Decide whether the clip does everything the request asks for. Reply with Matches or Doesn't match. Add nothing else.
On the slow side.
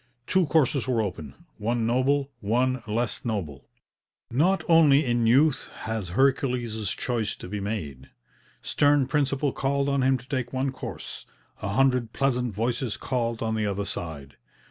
Doesn't match